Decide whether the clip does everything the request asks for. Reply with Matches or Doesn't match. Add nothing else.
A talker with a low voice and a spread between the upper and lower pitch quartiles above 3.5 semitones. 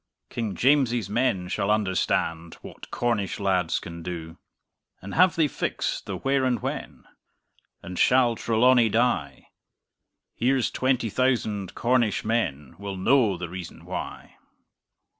Matches